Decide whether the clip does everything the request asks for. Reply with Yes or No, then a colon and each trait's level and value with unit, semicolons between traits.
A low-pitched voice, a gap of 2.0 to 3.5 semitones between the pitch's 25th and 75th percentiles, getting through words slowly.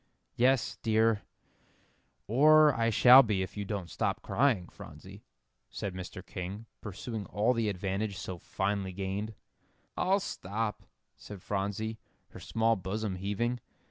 Yes: low, 105 Hz; average, 3.0 semitones; slow, 130 wpm